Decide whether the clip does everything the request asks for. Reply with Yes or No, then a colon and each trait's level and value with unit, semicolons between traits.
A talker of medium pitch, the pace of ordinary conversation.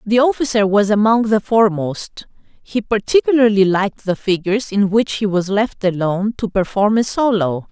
No: high, 210 Hz; average, 165 wpm